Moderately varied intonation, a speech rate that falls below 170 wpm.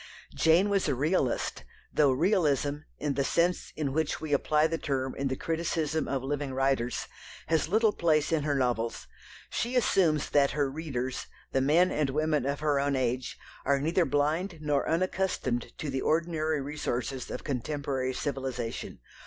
Yes: average, 3.1 semitones; average, 160 wpm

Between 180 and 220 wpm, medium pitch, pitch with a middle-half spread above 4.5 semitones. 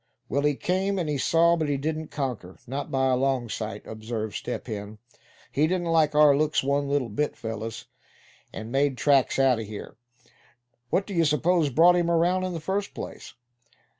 Yes: average, 185 wpm; medium, 145 Hz; average, 5.0 semitones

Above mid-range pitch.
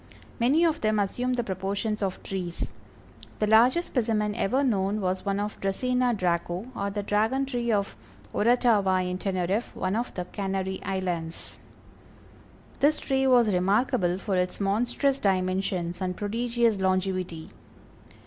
Yes: high, 200 Hz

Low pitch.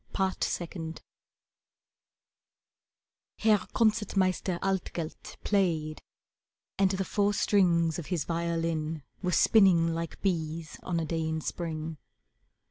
No: medium, 170 Hz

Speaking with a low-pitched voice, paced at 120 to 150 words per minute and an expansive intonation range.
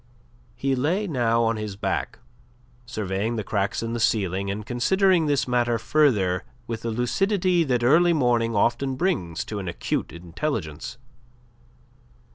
Yes: low, 120 Hz; average, 140 wpm; wide, 6.0 semitones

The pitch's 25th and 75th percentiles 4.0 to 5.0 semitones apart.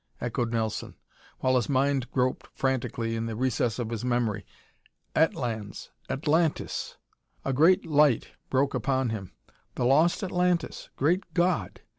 Yes: average, 4.6 semitones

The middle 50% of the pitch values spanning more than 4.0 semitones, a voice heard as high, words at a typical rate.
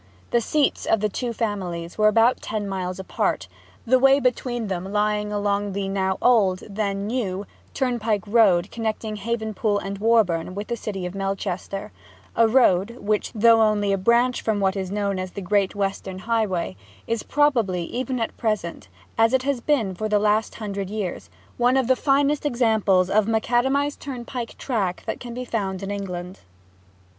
No: average, 3.3 semitones; high, 210 Hz; average, 175 wpm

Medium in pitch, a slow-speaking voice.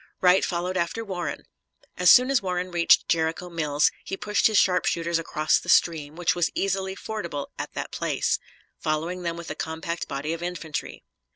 No: medium, 170 Hz; average, 175 wpm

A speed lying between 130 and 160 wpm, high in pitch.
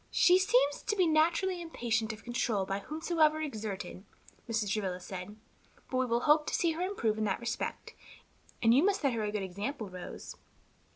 No: average, 185 wpm; high, 240 Hz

